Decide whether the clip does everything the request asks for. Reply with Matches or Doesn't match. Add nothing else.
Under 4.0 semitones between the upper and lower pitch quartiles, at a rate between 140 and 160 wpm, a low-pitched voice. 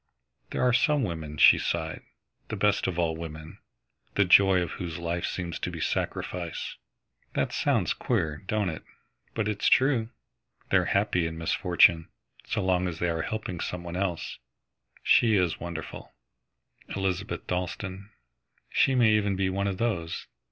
Matches